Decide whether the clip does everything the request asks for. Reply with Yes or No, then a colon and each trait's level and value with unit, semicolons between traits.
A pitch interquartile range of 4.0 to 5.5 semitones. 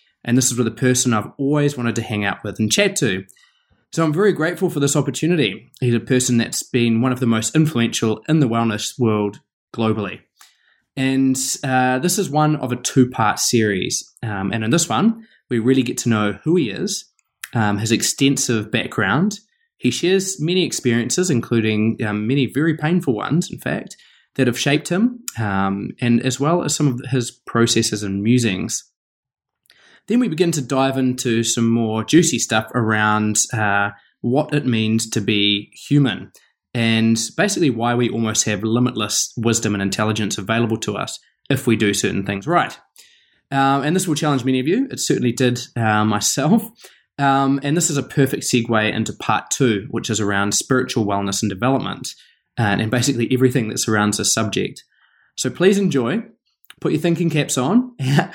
Yes: average, 4.6 semitones